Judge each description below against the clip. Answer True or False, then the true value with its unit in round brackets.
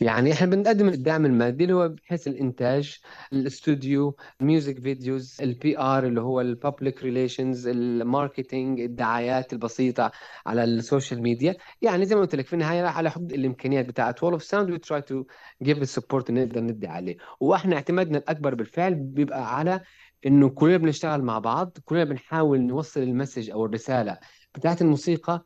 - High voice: False (135 Hz)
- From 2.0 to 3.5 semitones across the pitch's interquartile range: False (4.1 semitones)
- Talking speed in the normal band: False (150 wpm)